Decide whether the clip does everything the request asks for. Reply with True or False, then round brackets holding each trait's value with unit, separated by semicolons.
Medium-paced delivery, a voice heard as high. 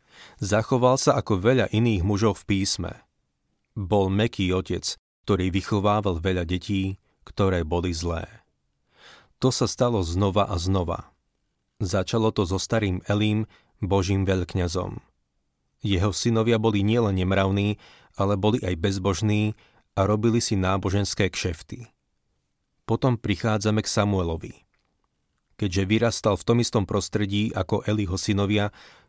False (120 wpm; 100 Hz)